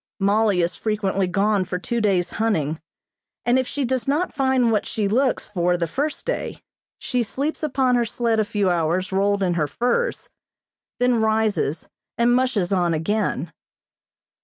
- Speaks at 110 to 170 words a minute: Yes, average, 160 wpm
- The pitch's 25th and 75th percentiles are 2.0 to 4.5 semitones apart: No, average, 5.0 semitones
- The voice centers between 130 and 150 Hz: No, high, 215 Hz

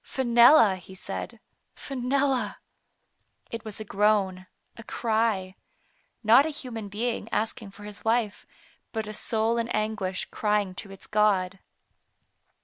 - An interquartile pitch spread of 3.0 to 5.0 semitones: No, narrow, 2.6 semitones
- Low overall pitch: No, high, 215 Hz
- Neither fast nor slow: No, slow, 130 wpm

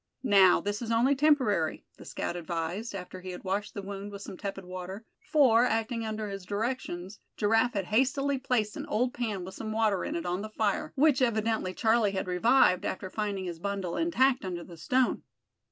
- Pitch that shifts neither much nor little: Yes, average, 4.1 semitones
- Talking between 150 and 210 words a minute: Yes, average, 195 wpm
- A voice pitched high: Yes, high, 210 Hz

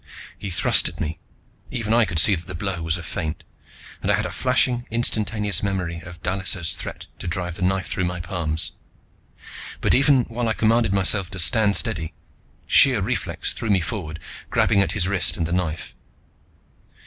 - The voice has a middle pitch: No, very low, 95 Hz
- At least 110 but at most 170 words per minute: No, average, 185 wpm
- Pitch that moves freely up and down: No, average, 3.9 semitones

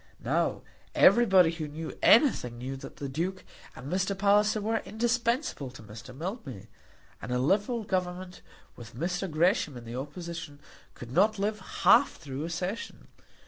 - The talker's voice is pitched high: No, medium, 180 Hz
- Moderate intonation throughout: No, wide, 6.9 semitones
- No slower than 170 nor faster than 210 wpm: No, average, 150 wpm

